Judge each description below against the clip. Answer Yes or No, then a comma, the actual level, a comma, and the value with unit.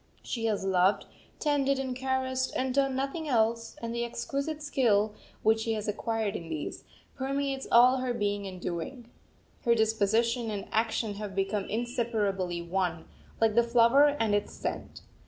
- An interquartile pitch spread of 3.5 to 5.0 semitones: Yes, average, 4.1 semitones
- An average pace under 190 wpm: Yes, average, 155 wpm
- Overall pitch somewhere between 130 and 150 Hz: No, high, 230 Hz